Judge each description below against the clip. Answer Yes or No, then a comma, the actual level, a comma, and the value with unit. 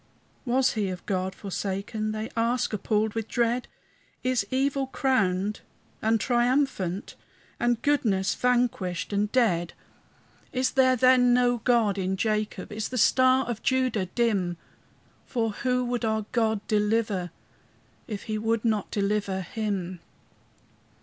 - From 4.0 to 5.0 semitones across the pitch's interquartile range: No, average, 3.6 semitones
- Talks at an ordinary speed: No, slow, 130 wpm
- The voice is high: Yes, high, 220 Hz